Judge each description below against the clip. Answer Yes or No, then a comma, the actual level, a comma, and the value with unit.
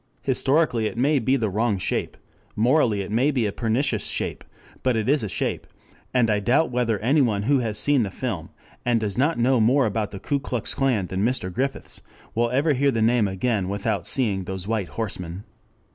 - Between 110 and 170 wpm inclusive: No, average, 200 wpm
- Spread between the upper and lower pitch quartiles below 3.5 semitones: No, average, 4.2 semitones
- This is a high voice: No, low, 115 Hz